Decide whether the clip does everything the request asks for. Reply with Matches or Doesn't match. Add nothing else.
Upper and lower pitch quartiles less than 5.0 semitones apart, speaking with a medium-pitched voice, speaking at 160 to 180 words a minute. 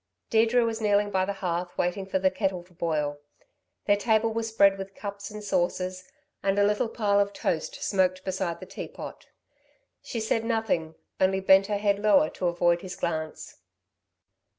Doesn't match